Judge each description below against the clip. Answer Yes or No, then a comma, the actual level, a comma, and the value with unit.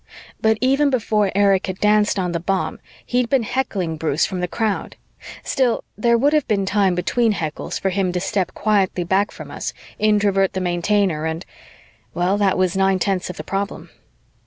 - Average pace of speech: Yes, average, 185 wpm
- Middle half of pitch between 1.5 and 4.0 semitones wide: Yes, average, 2.8 semitones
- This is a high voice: Yes, high, 195 Hz